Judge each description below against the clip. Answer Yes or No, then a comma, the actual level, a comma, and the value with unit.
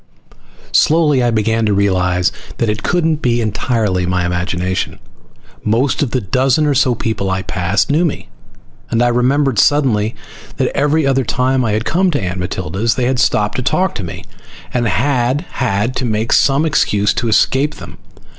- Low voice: Yes, low, 120 Hz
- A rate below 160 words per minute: No, average, 180 wpm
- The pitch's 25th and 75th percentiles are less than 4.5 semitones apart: No, average, 5.1 semitones